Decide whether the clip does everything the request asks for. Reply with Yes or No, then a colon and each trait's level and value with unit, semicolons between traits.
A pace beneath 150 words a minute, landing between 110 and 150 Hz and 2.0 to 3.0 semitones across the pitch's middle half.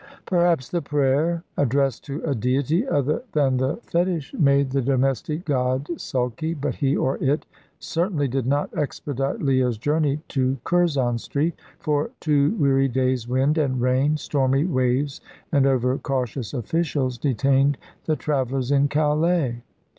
Yes: average, 140 wpm; medium, 140 Hz; narrow, 2.6 semitones